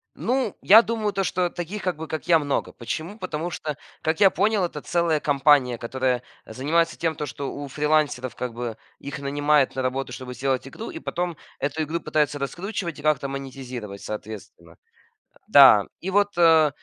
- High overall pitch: No, medium, 150 Hz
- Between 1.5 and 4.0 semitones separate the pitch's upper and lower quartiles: No, average, 4.7 semitones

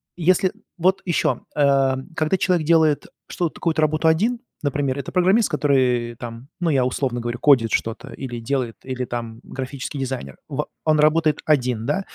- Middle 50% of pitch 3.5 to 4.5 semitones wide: Yes, average, 4.2 semitones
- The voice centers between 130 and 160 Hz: Yes, medium, 140 Hz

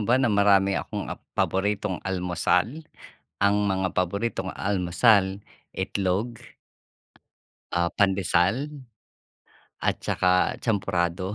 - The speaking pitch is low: Yes, very low, 95 Hz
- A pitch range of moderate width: No, narrow, 2.0 semitones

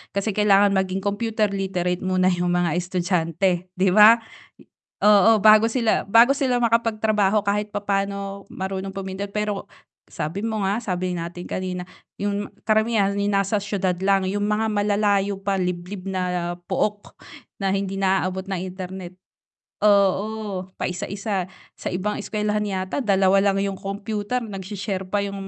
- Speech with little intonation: Yes, narrow, 1.9 semitones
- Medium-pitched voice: No, high, 195 Hz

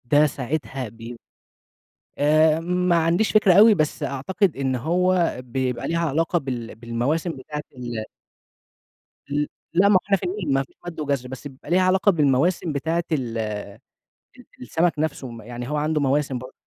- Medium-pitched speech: Yes, medium, 150 Hz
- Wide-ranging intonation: No, average, 5.0 semitones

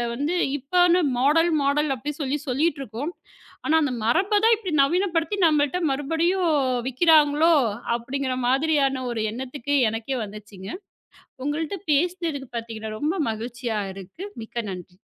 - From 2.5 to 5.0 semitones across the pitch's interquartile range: No, wide, 5.4 semitones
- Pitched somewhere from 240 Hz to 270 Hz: No, very high, 285 Hz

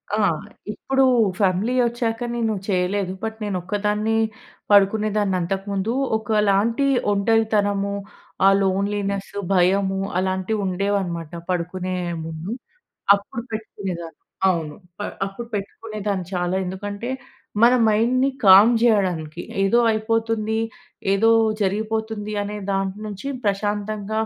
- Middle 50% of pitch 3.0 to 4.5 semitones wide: No, narrow, 2.4 semitones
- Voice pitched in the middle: No, high, 205 Hz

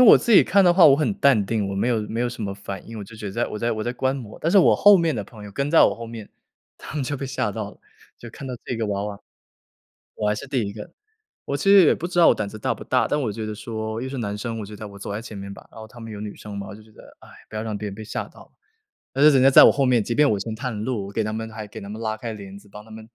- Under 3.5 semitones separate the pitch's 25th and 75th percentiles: No, average, 3.9 semitones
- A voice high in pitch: No, low, 110 Hz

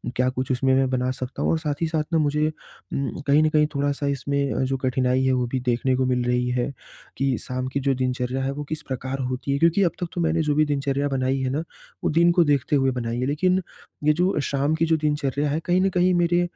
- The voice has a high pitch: No, medium, 140 Hz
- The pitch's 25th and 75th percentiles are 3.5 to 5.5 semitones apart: No, average, 3.0 semitones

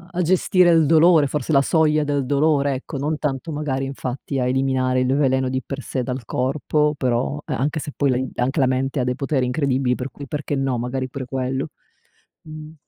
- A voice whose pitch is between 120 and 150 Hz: Yes, low, 135 Hz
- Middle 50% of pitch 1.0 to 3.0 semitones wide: Yes, narrow, 2.6 semitones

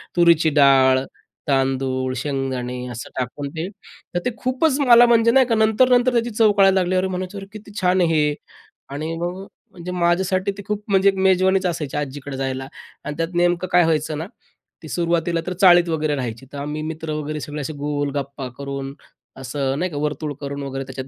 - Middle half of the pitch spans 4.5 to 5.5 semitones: Yes, average, 5.1 semitones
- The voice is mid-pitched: Yes, medium, 160 Hz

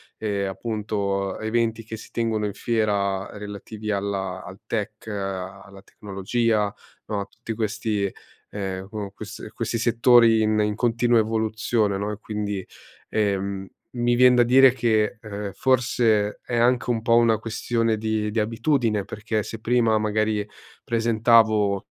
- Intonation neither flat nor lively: No, narrow, 2.1 semitones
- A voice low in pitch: Yes, low, 110 Hz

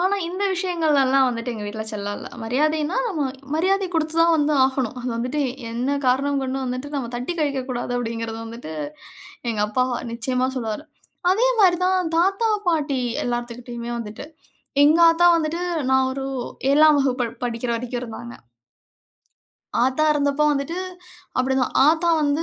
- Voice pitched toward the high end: Yes, very high, 275 Hz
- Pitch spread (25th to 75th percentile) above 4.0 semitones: Yes, average, 4.6 semitones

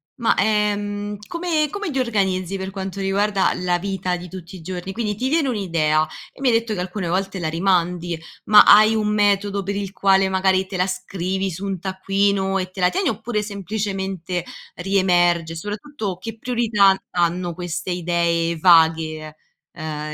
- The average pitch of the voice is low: No, high, 190 Hz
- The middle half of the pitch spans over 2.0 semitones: Yes, average, 2.7 semitones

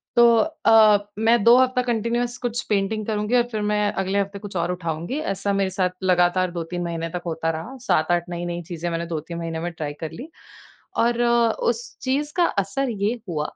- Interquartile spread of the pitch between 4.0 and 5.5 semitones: Yes, average, 5.1 semitones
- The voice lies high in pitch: Yes, high, 195 Hz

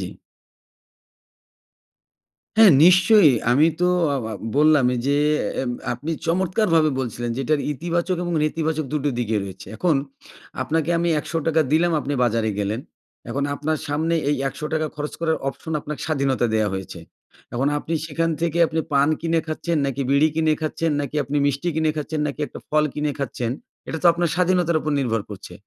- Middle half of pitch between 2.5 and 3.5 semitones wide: Yes, average, 3.1 semitones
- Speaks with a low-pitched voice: No, medium, 155 Hz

